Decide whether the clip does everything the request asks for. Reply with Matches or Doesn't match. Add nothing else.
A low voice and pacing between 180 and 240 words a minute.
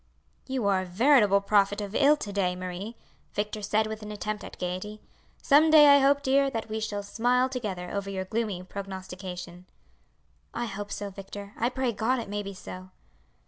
Doesn't match